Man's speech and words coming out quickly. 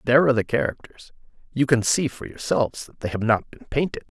Yes: male; fast, 215 wpm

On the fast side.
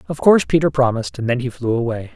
Yes: fast, 250 wpm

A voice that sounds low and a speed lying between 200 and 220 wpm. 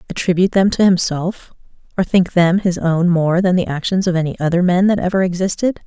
No: medium, 180 Hz; fast, 205 wpm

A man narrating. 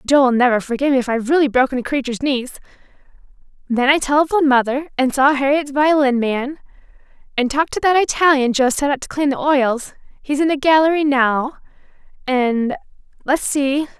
No: female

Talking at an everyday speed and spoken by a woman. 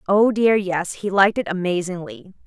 Yes: average, 170 wpm; female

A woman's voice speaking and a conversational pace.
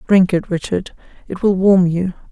Yes: female; average, 180 wpm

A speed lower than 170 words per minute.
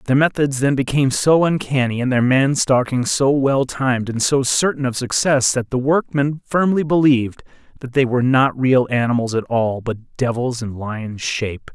No: average, 185 wpm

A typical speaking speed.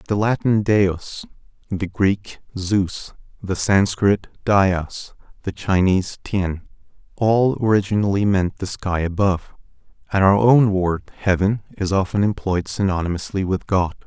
No: slow, 125 wpm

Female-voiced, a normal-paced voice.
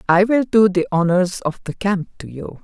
No: female; fast, 230 wpm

